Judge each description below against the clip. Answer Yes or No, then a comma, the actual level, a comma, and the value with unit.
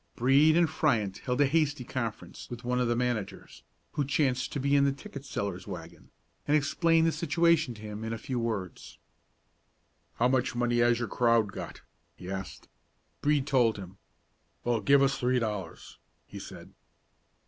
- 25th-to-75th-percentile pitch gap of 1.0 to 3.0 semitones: No, average, 3.8 semitones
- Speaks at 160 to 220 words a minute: Yes, average, 170 wpm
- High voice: No, low, 125 Hz